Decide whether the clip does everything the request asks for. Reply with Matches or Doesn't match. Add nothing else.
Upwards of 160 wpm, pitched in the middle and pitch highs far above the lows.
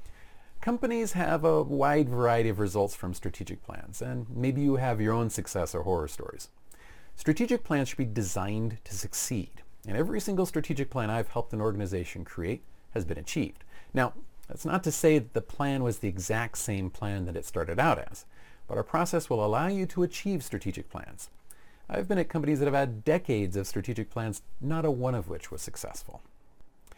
Doesn't match